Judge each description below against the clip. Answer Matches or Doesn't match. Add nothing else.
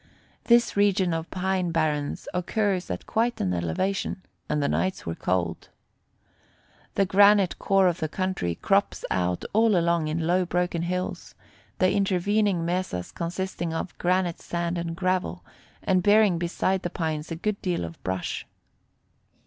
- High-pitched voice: Doesn't match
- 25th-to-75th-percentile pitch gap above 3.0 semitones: Doesn't match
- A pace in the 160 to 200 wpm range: Doesn't match